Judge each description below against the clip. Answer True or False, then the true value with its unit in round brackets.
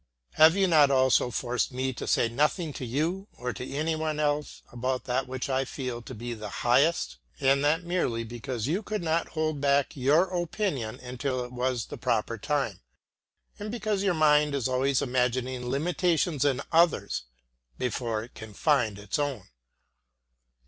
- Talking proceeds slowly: False (165 wpm)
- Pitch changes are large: False (4.2 semitones)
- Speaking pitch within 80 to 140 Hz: True (135 Hz)